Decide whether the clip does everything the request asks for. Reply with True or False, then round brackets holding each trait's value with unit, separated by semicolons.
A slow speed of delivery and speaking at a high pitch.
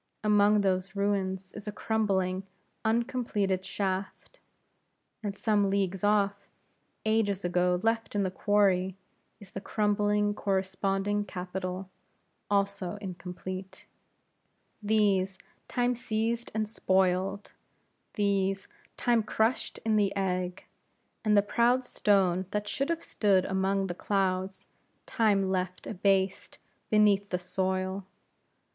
True (110 wpm; 195 Hz)